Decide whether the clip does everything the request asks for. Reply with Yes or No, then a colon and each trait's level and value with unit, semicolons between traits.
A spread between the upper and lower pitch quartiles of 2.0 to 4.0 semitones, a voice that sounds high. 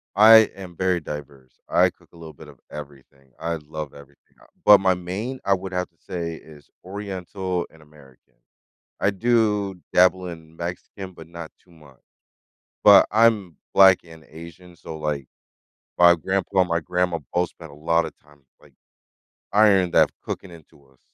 No: average, 3.5 semitones; very low, 85 Hz